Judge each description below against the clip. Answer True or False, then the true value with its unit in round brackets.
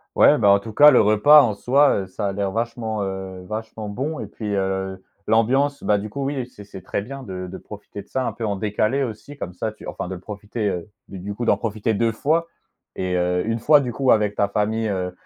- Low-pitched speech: True (105 Hz)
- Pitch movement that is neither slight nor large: True (3.6 semitones)